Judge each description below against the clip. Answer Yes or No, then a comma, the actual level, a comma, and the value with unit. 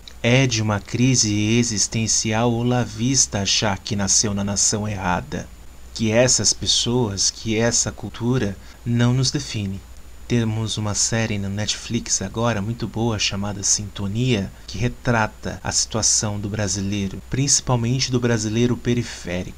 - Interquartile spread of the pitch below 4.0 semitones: Yes, average, 3.0 semitones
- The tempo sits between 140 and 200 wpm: No, average, 130 wpm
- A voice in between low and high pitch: No, low, 110 Hz